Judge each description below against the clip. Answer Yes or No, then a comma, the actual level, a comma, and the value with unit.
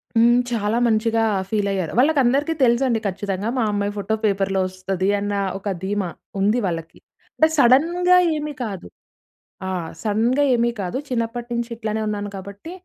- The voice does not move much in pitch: No, average, 3.4 semitones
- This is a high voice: Yes, high, 220 Hz